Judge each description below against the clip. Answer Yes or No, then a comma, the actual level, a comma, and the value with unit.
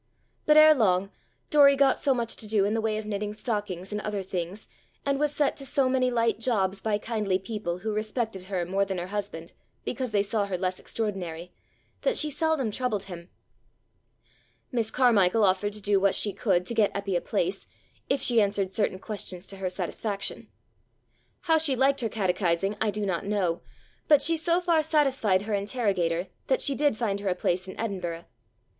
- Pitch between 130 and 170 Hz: No, high, 210 Hz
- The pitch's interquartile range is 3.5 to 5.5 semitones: Yes, average, 4.6 semitones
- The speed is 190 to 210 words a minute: Yes, average, 195 wpm